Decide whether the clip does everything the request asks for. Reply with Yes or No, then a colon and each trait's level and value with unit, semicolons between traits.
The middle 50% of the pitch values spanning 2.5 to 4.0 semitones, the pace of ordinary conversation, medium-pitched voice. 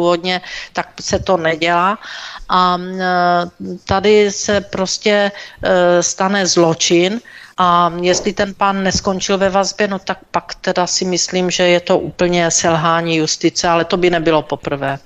No: narrow, 2.1 semitones; average, 135 wpm; medium, 180 Hz